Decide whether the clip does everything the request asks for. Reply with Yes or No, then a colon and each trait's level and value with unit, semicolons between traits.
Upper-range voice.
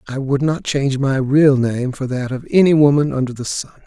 No: low, 135 Hz